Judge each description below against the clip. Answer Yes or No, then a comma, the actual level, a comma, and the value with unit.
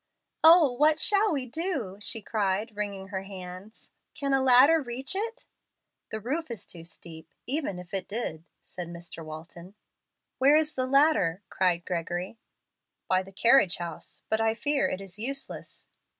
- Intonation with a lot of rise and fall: Yes, wide, 7.1 semitones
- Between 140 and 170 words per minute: Yes, average, 160 wpm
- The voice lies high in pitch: Yes, high, 215 Hz